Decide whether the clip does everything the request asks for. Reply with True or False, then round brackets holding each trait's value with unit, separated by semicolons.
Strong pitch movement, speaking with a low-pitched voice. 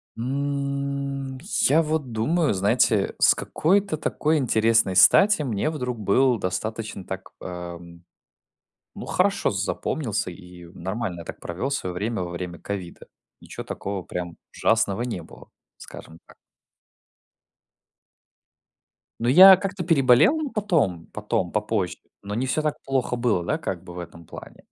True (7.1 semitones; 115 Hz)